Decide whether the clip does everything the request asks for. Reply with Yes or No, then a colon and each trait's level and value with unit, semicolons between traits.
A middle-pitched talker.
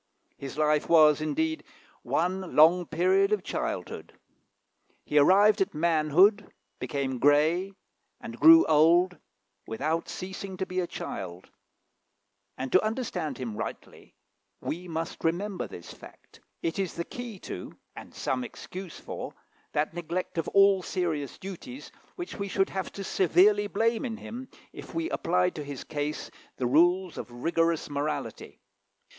Yes: medium, 175 Hz